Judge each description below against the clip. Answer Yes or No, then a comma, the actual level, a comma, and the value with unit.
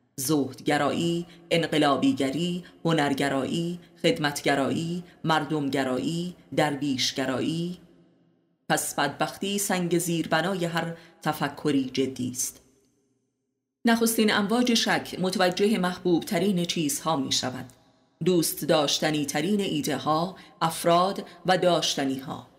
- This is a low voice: No, medium, 160 Hz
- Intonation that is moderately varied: Yes, average, 4.3 semitones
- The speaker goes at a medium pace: No, slow, 90 wpm